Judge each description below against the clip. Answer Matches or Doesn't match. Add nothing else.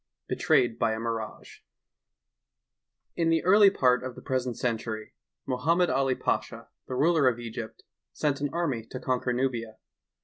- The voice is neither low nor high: Doesn't match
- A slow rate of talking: Doesn't match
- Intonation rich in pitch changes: Doesn't match